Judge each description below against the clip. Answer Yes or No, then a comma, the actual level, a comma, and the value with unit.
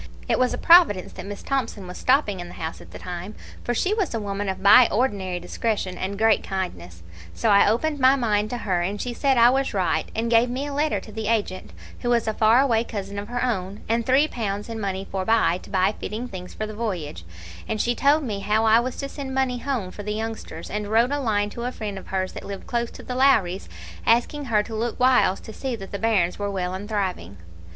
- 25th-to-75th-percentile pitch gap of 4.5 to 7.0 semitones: No, average, 3.9 semitones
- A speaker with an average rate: No, fast, 245 wpm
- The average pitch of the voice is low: No, high, 215 Hz